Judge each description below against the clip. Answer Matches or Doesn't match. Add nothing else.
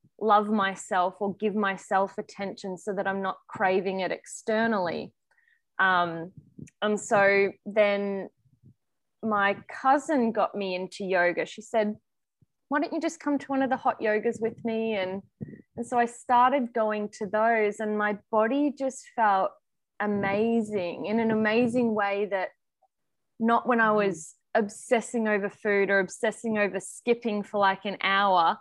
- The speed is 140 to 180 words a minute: Matches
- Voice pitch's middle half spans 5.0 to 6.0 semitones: Doesn't match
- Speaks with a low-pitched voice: Doesn't match